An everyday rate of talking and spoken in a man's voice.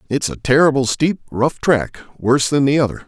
Yes: average, 195 wpm; male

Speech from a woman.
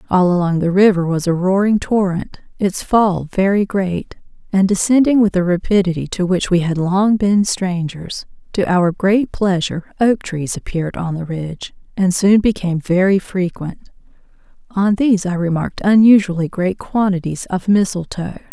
Yes: female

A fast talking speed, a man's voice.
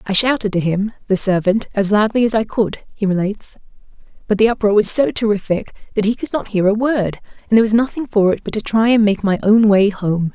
No: fast, 240 wpm; female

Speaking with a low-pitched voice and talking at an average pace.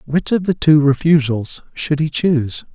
No: medium, 150 Hz; average, 175 wpm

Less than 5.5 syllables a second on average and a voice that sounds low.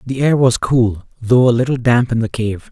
Yes: 5.0 syllables/s; low, 120 Hz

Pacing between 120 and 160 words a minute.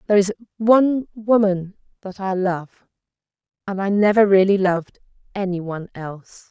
Yes: average, 140 wpm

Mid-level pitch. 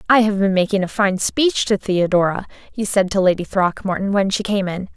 No: high, 195 Hz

